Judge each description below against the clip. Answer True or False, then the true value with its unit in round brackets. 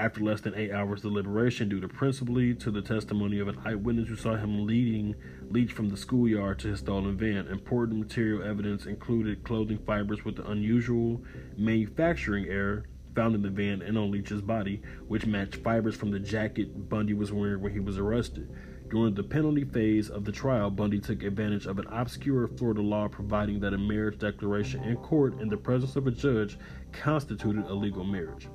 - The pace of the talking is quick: False (190 wpm)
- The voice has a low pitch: True (105 Hz)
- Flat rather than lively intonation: True (2.0 semitones)